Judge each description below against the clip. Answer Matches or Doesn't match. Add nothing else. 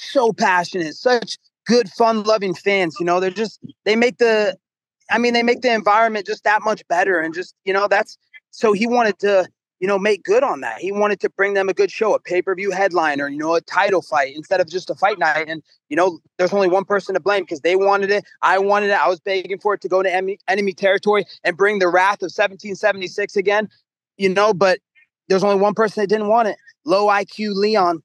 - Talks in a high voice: Matches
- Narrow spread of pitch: Matches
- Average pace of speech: Doesn't match